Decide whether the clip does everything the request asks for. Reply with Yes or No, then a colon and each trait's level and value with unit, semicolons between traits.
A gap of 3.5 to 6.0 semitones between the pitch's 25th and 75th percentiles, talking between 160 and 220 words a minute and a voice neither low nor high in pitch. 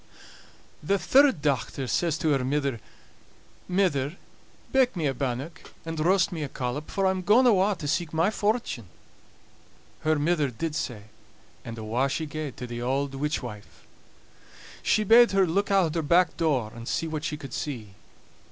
Yes: wide, 5.5 semitones; average, 170 wpm; medium, 155 Hz